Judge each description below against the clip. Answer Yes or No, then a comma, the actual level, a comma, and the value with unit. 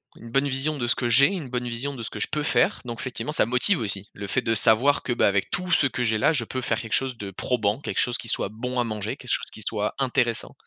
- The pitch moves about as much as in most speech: Yes, average, 3.4 semitones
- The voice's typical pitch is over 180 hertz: No, low, 120 Hz